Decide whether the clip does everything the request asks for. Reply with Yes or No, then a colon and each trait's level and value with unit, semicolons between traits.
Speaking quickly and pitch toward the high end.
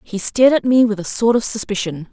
Yes: fast, 255 wpm; high, 220 Hz